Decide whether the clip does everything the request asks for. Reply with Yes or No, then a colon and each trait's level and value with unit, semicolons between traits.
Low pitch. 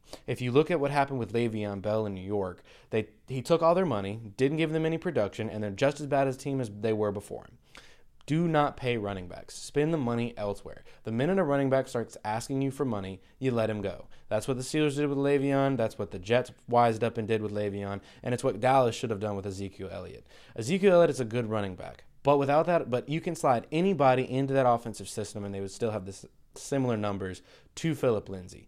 Yes: low, 120 Hz